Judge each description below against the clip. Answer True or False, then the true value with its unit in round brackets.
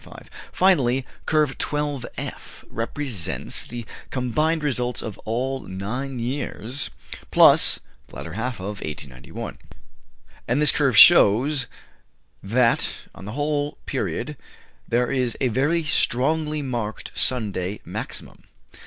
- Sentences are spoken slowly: True (110 wpm)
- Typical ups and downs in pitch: True (4.5 semitones)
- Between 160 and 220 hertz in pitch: False (125 Hz)